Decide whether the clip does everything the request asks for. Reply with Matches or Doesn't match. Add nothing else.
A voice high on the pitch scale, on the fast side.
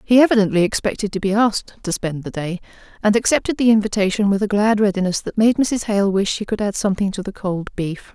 Matches